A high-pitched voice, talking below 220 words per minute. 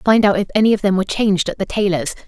No: high, 195 Hz; fast, 290 wpm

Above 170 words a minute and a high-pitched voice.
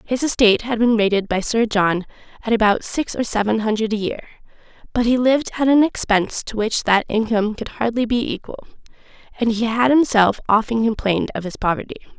Yes: average, 190 wpm; high, 225 Hz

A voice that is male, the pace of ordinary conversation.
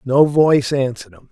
Yes: male; average, 180 wpm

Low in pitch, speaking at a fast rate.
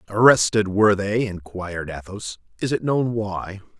No: low, 100 Hz; average, 140 wpm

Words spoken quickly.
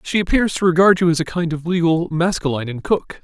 Yes: fast, 240 wpm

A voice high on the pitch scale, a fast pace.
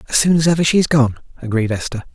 No: medium, 140 Hz; fast, 225 wpm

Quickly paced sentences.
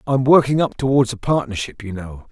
Yes: fast, 235 wpm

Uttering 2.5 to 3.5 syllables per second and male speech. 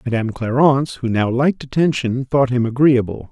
No: 5.7 syllables/s; male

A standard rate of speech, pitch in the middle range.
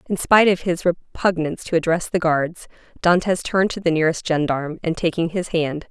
Yes: average, 195 wpm; medium, 170 Hz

